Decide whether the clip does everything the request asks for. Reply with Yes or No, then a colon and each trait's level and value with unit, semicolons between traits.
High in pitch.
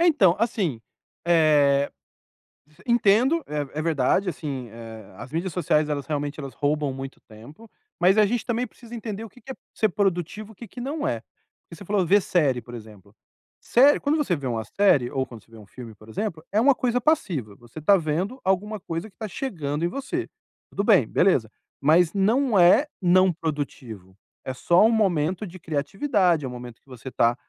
No: medium, 170 Hz